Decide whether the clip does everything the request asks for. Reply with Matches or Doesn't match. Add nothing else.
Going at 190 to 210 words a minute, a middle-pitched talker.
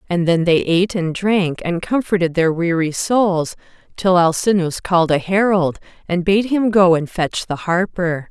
Doesn't match